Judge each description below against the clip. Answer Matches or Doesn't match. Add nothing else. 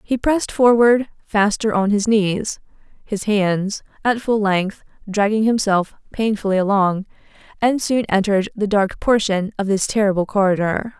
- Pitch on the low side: Doesn't match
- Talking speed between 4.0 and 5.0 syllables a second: Matches